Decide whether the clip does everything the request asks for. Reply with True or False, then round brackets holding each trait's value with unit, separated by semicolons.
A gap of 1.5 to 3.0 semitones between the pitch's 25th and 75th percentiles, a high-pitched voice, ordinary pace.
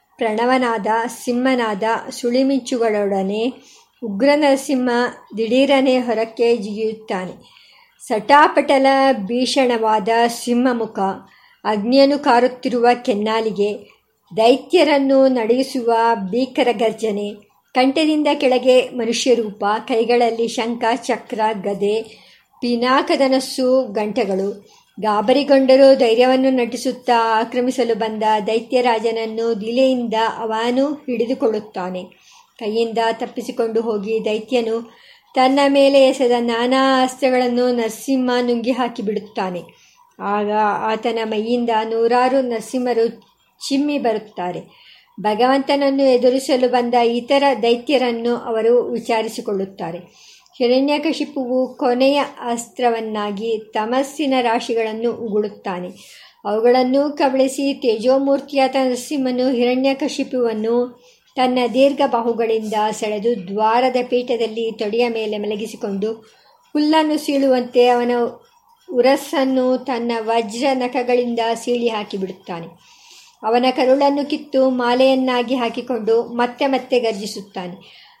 True (2.7 semitones; 240 Hz; 80 wpm)